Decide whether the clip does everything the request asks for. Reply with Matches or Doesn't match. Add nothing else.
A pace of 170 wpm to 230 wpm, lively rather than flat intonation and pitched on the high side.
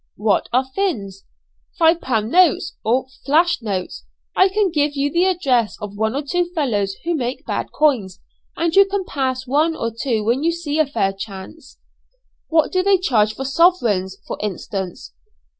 Matches